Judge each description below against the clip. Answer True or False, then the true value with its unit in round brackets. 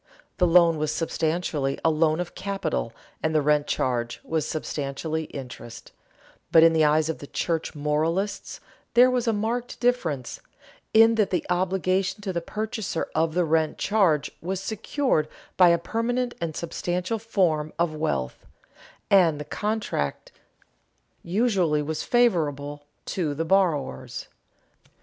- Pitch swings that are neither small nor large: True (4.4 semitones)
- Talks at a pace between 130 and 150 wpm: True (140 wpm)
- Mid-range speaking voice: True (165 Hz)